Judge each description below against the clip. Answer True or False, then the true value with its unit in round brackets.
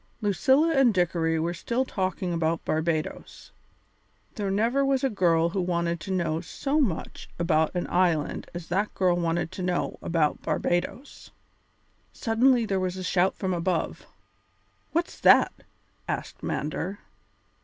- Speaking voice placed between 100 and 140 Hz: False (180 Hz)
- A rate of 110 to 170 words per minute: True (140 wpm)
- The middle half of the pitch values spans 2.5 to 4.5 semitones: True (4.2 semitones)